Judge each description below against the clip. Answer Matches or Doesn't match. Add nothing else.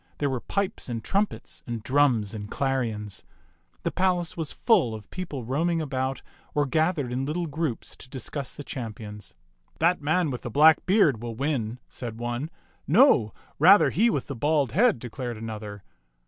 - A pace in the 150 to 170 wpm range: Matches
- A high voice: Doesn't match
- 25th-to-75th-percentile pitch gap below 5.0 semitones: Doesn't match